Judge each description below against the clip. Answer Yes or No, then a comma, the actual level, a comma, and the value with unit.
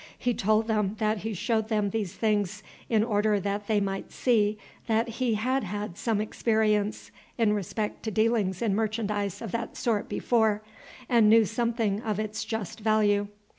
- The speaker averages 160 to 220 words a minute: Yes, average, 170 wpm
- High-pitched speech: Yes, high, 215 Hz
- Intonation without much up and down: Yes, narrow, 1.5 semitones